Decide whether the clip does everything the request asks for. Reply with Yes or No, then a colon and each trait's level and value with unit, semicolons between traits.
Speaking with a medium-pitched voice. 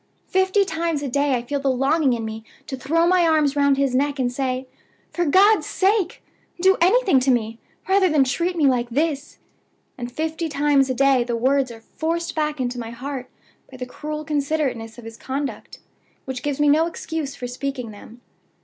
No: very high, 280 Hz